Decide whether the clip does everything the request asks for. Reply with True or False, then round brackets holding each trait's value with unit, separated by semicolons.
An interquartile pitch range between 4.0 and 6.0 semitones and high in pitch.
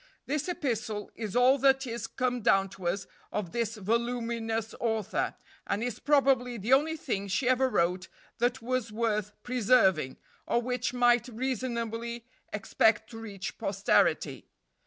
False (2.9 semitones; 235 Hz)